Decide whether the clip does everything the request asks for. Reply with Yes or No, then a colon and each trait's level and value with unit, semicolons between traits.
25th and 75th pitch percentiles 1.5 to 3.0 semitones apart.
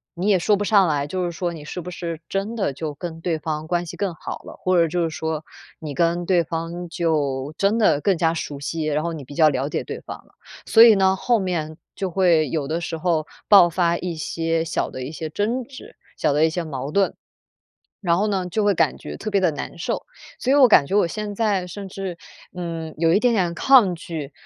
No: average, 3.6 semitones